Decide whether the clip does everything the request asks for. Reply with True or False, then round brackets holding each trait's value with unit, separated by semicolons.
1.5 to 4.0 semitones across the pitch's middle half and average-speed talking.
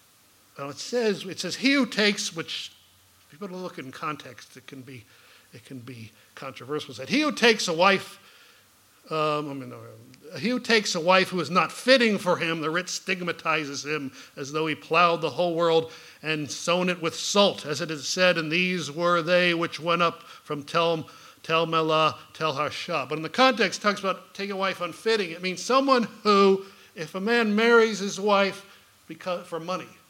False (4.4 semitones; 195 wpm)